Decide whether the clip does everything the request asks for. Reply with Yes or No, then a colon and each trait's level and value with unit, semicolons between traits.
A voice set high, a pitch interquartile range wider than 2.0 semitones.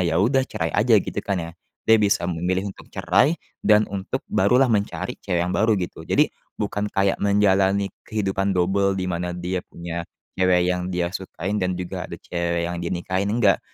No: very low, 95 Hz; narrow, 2.4 semitones